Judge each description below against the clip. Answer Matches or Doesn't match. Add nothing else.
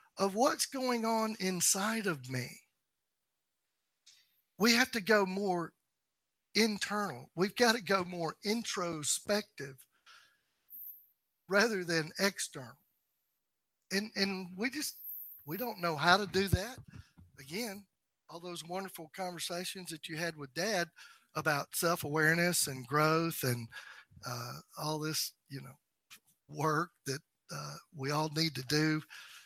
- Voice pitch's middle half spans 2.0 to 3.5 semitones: Doesn't match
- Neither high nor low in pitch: Matches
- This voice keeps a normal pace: Doesn't match